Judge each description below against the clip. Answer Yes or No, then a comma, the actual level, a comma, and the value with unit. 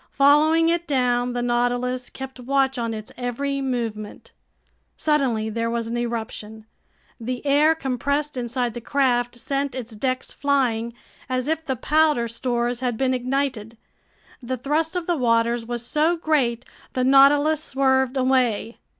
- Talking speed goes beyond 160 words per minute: No, average, 145 wpm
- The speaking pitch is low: No, very high, 255 Hz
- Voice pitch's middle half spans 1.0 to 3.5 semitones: Yes, average, 2.9 semitones